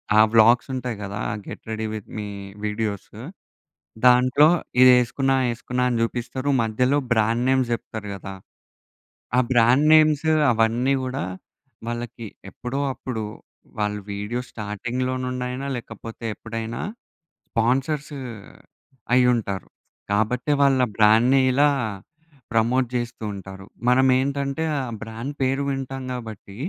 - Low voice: Yes, low, 120 Hz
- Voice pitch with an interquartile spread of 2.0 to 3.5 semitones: Yes, average, 3.0 semitones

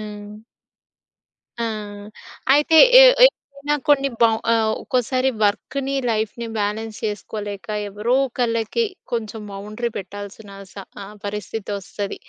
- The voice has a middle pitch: No, high, 220 Hz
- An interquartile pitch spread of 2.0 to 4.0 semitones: Yes, average, 3.7 semitones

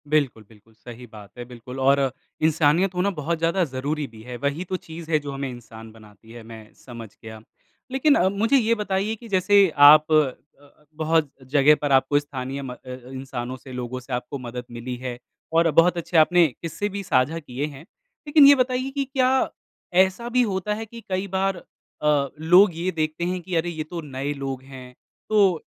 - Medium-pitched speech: Yes, medium, 150 Hz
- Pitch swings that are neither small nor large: No, wide, 6.5 semitones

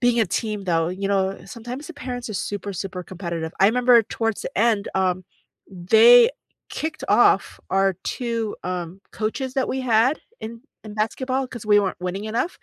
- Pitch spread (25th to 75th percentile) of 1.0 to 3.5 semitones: No, average, 4.1 semitones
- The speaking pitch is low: No, high, 215 Hz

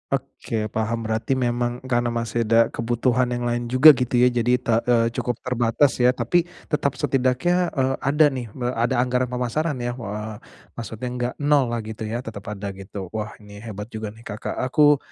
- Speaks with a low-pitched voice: Yes, low, 120 Hz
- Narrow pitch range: Yes, narrow, 2.2 semitones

